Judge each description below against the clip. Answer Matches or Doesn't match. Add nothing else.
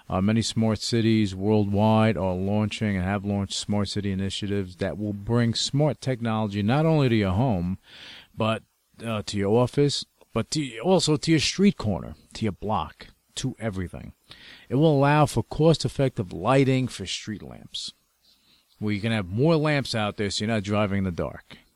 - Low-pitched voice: Matches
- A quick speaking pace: Doesn't match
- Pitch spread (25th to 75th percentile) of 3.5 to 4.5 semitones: Matches